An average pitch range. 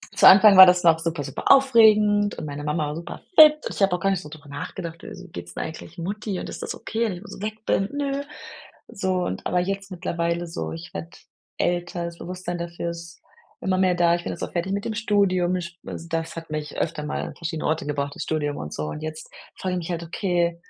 Yes: average, 3.0 semitones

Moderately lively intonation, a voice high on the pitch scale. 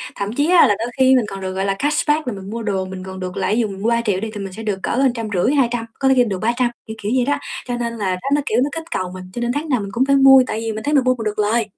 Yes: average, 4.4 semitones; high, 230 Hz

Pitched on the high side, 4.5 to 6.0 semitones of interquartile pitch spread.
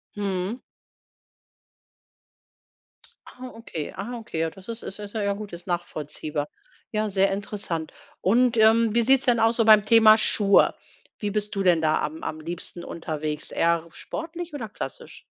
Yes: high, 205 Hz; average, 4.9 semitones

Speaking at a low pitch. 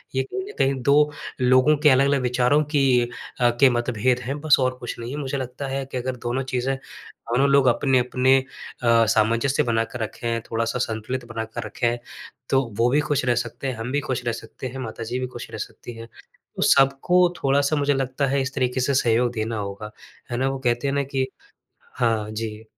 Yes: low, 130 Hz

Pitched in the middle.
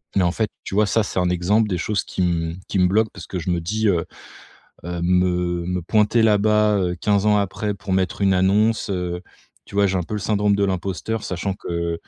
No: very low, 95 Hz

